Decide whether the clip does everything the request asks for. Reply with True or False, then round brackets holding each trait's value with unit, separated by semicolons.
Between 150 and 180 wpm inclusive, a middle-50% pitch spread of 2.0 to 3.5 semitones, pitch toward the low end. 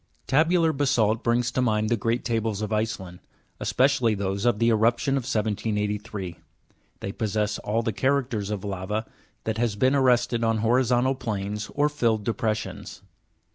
True (155 wpm; 2.9 semitones; 115 Hz)